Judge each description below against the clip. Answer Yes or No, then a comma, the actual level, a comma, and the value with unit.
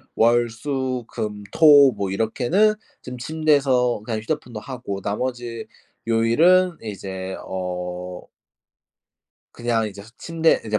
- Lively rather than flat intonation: No, average, 4.8 semitones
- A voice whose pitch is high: No, low, 120 Hz